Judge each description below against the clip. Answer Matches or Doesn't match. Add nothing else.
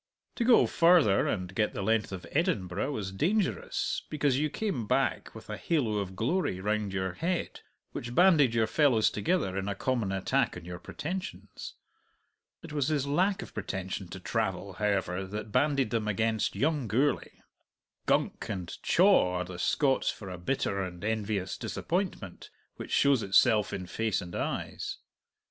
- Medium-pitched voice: Doesn't match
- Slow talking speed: Doesn't match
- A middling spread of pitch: Doesn't match